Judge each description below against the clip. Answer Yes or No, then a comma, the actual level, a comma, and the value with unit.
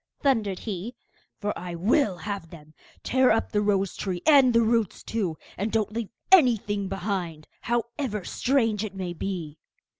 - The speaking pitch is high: Yes, high, 205 Hz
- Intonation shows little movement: No, average, 3.9 semitones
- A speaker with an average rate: Yes, average, 155 wpm